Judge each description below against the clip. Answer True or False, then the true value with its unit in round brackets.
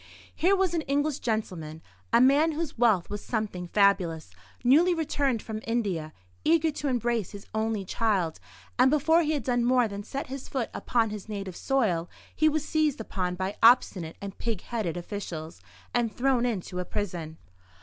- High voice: True (225 Hz)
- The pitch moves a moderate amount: False (6.3 semitones)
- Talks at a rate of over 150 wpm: True (170 wpm)